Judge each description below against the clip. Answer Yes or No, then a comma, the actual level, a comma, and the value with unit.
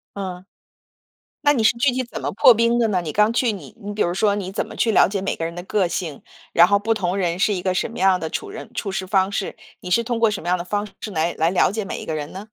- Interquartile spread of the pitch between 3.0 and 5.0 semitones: Yes, average, 3.3 semitones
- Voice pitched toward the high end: Yes, high, 195 Hz